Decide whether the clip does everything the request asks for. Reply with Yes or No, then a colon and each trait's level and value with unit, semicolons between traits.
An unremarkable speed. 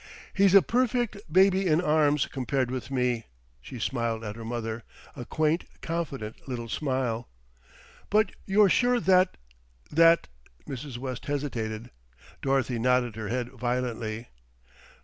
No: slow, 130 wpm